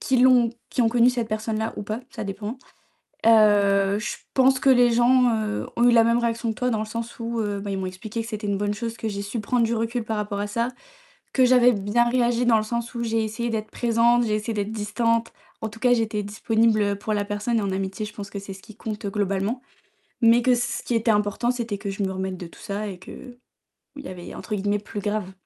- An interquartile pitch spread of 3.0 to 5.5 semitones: No, narrow, 2.4 semitones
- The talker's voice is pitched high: Yes, high, 220 Hz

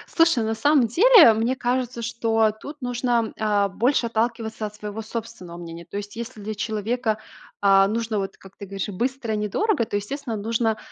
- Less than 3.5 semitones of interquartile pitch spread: Yes, average, 2.7 semitones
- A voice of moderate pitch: No, high, 225 Hz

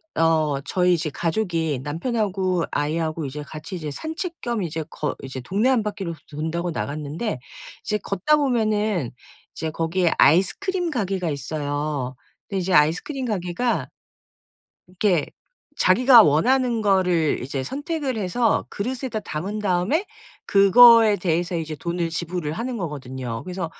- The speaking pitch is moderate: Yes, medium, 180 Hz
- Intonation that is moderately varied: No, wide, 5.8 semitones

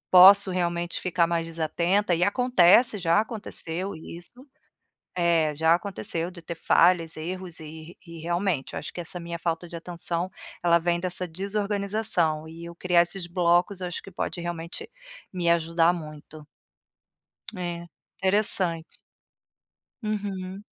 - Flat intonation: Yes, narrow, 2.0 semitones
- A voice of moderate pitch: Yes, medium, 175 Hz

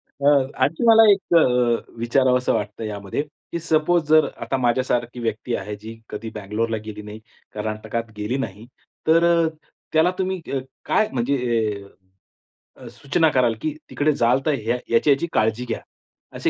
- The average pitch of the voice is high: No, low, 125 Hz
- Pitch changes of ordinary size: No, wide, 5.7 semitones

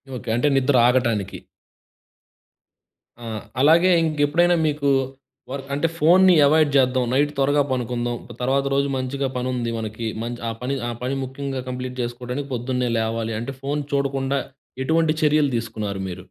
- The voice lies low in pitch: Yes, low, 130 Hz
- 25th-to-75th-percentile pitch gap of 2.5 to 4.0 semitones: Yes, average, 3.1 semitones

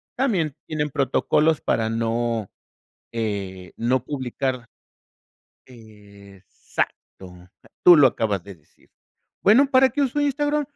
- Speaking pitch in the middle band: No, low, 120 Hz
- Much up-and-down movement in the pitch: Yes, wide, 7.9 semitones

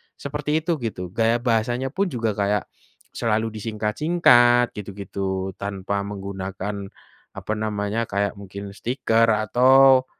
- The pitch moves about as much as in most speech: Yes, average, 3.4 semitones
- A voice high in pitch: No, low, 110 Hz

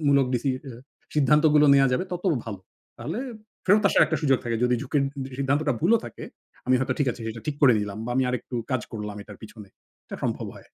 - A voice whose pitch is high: No, low, 135 Hz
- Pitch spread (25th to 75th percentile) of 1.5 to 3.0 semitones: No, average, 4.2 semitones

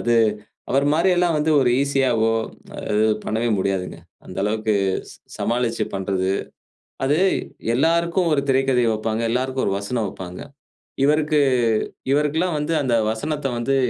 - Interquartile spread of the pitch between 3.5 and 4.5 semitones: No, average, 5.2 semitones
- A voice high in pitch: No, low, 130 Hz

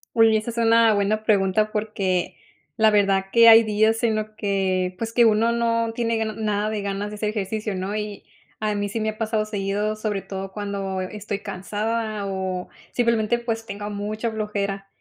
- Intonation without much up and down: Yes, narrow, 1.9 semitones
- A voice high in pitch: Yes, high, 215 Hz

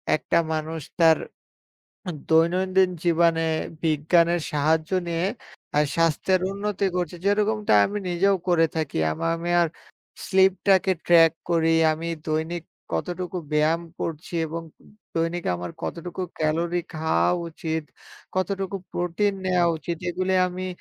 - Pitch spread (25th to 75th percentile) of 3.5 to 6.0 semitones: No, narrow, 2.4 semitones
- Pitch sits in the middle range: Yes, medium, 170 Hz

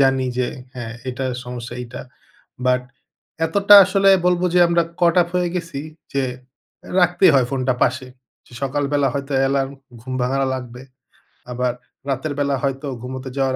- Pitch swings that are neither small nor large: Yes, average, 3.7 semitones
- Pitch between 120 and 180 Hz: Yes, low, 135 Hz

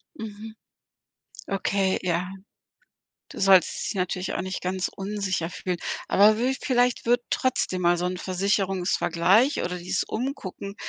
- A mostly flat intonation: No, average, 3.0 semitones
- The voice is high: Yes, high, 195 Hz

